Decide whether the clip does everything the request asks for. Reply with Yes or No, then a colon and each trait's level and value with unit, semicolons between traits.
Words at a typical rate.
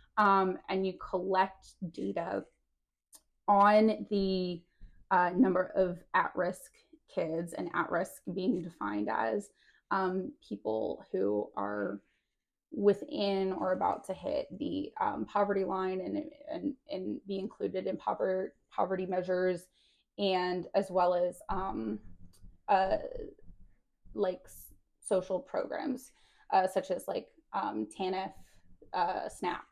No: slow, 110 wpm